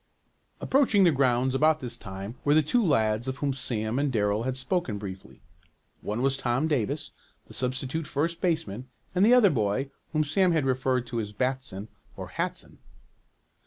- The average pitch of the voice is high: No, low, 130 Hz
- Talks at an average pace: Yes, average, 170 wpm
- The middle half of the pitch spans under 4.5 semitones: No, average, 5.1 semitones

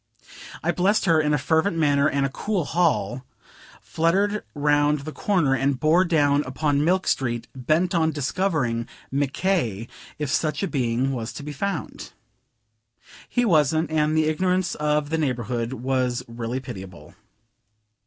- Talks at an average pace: Yes, average, 150 wpm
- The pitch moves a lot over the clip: No, average, 4.2 semitones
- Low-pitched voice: No, medium, 150 Hz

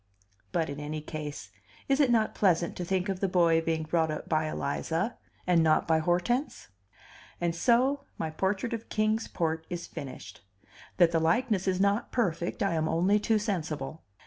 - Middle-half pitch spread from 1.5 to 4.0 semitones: No, average, 4.5 semitones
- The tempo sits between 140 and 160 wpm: No, average, 175 wpm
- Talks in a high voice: No, medium, 175 Hz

